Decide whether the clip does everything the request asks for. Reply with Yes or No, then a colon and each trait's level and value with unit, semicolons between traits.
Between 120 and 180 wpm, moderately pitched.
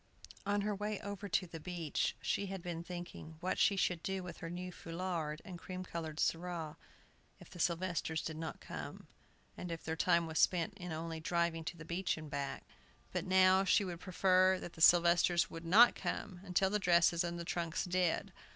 No: average, 195 wpm; medium, 175 Hz